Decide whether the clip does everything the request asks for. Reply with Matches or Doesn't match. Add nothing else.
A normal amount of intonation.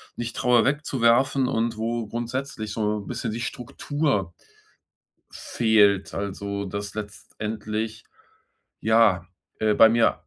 Doesn't match